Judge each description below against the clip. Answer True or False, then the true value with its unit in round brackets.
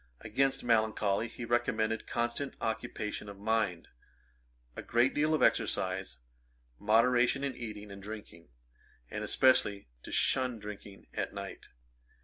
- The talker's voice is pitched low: True (110 Hz)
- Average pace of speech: False (125 wpm)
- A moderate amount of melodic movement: True (3.1 semitones)